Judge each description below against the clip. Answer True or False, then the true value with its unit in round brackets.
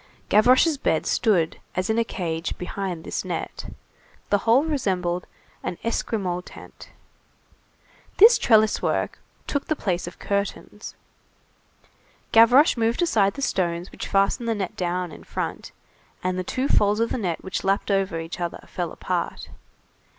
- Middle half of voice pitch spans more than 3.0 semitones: True (4.4 semitones)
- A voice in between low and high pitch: False (200 Hz)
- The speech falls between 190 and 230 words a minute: False (150 wpm)